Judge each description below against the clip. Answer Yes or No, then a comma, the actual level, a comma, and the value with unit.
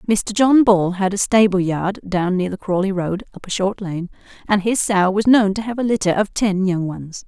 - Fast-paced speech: Yes, fast, 240 wpm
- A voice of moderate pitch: No, high, 195 Hz